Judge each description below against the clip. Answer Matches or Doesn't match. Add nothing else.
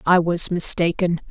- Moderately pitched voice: Matches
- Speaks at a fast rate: Doesn't match